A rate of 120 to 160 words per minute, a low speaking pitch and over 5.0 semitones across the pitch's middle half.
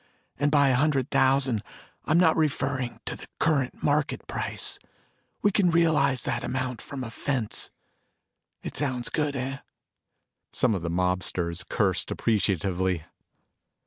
Yes: average, 140 wpm; low, 130 Hz; wide, 5.5 semitones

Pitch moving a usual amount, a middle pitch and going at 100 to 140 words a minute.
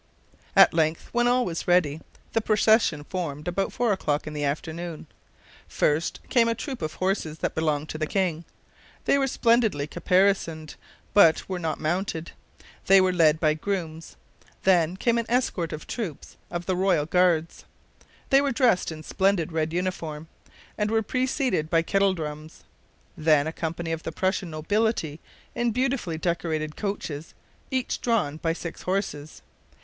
No: average, 4.5 semitones; medium, 175 Hz; average, 155 wpm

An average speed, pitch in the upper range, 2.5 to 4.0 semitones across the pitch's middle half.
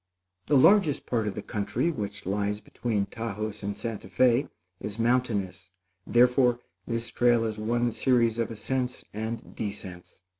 No: average, 145 wpm; low, 115 Hz; average, 2.9 semitones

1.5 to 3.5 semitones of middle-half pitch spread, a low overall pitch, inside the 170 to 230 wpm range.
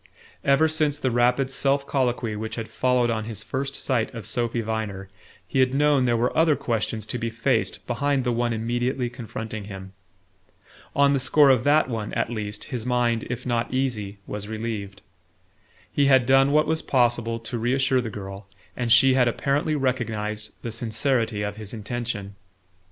Yes: average, 3.2 semitones; low, 120 Hz; average, 175 wpm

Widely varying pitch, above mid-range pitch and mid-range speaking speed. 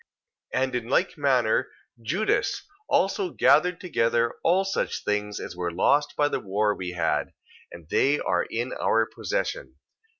No: wide, 8.0 semitones; low, 130 Hz; average, 155 wpm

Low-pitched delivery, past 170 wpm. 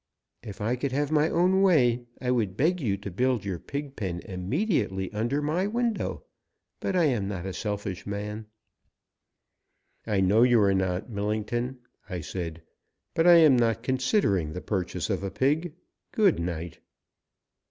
No: low, 115 Hz; average, 160 wpm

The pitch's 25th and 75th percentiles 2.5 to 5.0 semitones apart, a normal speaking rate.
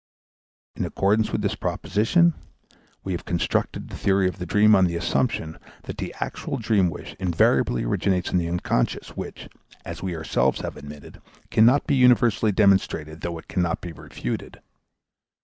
Yes: average, 4.3 semitones; average, 160 wpm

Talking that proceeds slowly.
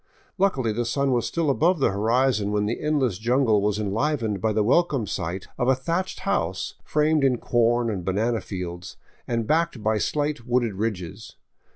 No: average, 175 wpm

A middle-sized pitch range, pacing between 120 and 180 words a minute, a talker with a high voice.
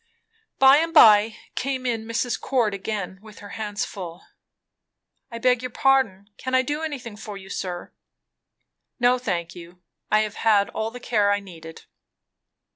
Yes: average, 4.1 semitones; average, 160 wpm; high, 220 Hz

